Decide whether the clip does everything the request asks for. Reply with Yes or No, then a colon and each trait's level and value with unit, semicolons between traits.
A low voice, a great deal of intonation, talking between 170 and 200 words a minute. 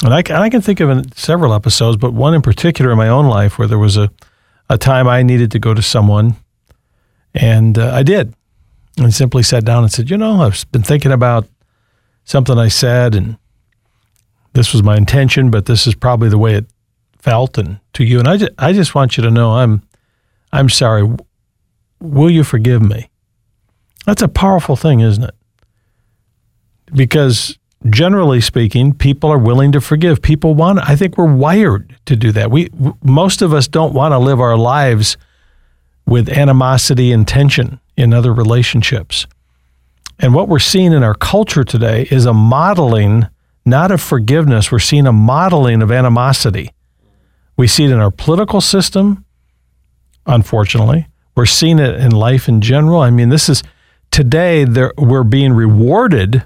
No: low, 120 Hz; average, 4.1 semitones; average, 175 wpm